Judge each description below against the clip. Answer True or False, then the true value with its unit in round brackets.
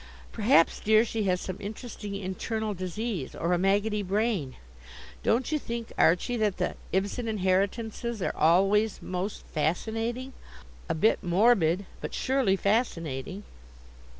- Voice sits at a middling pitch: False (205 Hz)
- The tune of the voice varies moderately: True (3.5 semitones)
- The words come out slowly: True (125 wpm)